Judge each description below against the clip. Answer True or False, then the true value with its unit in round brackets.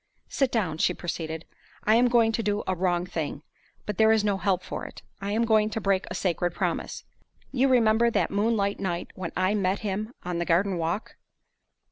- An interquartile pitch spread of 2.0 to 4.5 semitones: True (3.7 semitones)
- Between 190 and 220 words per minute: True (200 wpm)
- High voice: True (200 Hz)